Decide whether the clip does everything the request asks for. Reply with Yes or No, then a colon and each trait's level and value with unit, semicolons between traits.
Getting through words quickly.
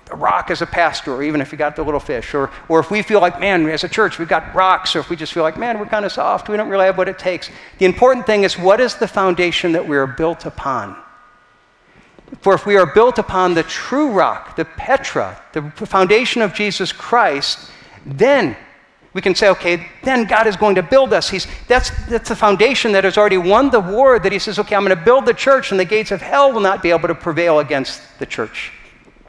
Yes: fast, 245 wpm